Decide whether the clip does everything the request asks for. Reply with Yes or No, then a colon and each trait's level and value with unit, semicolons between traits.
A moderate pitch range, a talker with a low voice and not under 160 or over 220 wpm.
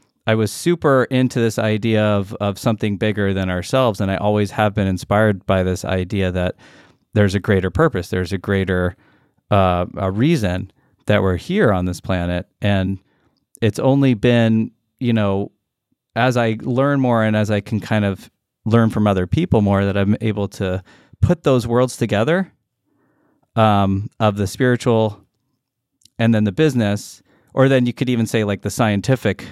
Yes: average, 3.4 semitones; low, 105 Hz; average, 170 wpm